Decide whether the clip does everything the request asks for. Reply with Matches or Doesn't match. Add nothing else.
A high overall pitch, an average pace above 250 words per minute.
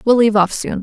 Matches